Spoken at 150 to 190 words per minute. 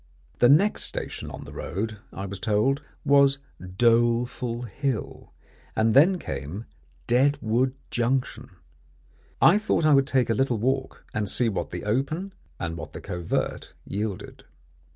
No: average, 140 wpm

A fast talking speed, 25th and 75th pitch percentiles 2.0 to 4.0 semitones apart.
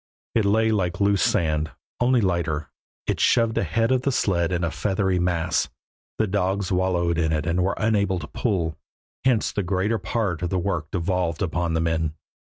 No: average, 180 wpm; average, 3.5 semitones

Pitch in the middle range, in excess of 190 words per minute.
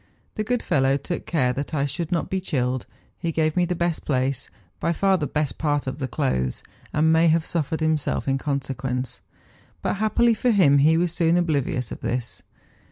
Yes: medium, 155 Hz; average, 200 wpm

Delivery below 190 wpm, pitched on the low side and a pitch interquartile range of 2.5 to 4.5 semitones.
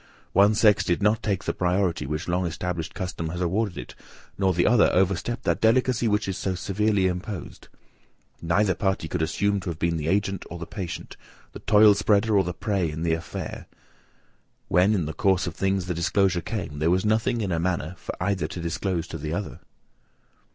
No: average, 200 wpm; very low, 95 Hz; average, 3.2 semitones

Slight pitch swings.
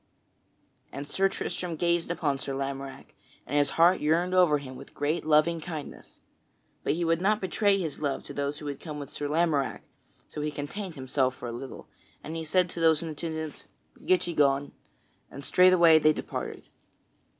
No: average, 3.3 semitones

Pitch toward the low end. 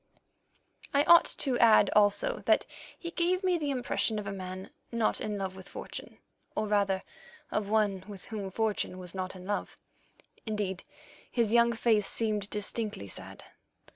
No: high, 210 Hz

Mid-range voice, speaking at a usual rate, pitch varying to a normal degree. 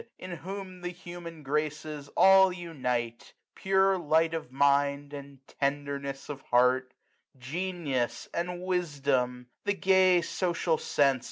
No: medium, 150 Hz; slow, 120 wpm; average, 4.4 semitones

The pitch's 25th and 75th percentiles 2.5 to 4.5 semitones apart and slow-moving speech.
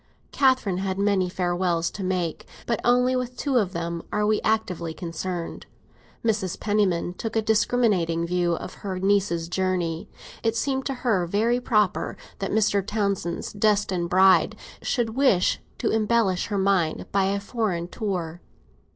No: average, 3.8 semitones; average, 150 wpm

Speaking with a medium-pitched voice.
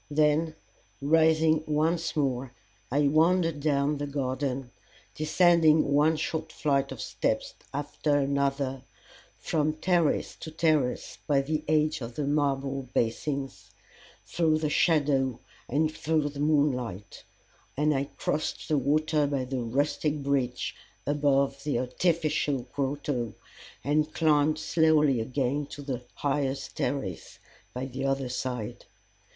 Yes: medium, 145 Hz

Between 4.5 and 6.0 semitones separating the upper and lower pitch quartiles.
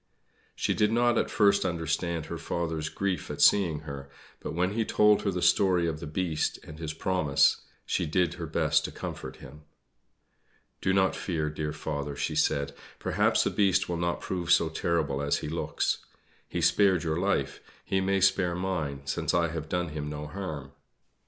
No: average, 3.6 semitones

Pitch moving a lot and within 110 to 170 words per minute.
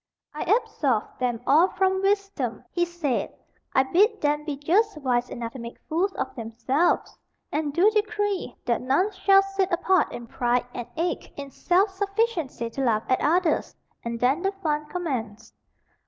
Yes: wide, 7.4 semitones; average, 165 wpm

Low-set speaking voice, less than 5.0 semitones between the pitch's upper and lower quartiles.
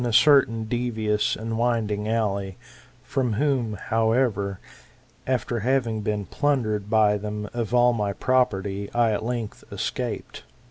Yes: low, 110 Hz; average, 2.7 semitones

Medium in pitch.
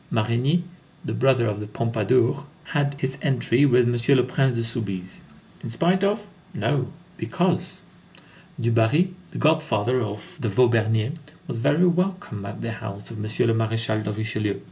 No: low, 120 Hz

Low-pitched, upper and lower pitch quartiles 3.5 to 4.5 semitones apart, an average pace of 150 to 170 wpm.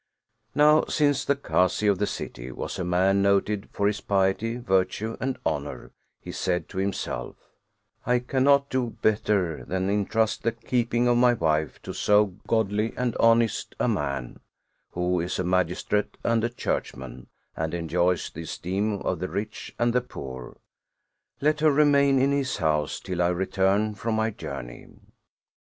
No: low, 105 Hz; average, 4.9 semitones; average, 160 wpm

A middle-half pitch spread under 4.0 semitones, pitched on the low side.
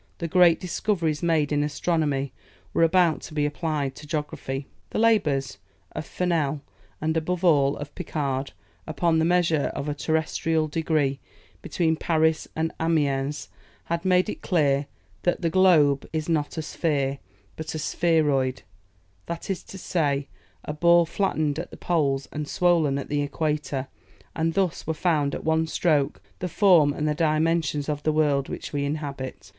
No: narrow, 2.6 semitones; medium, 155 Hz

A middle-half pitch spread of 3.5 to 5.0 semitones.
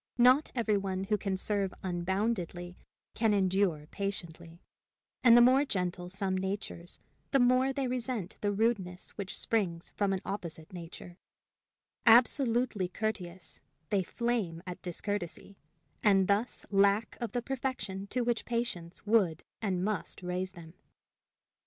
Yes: average, 4.3 semitones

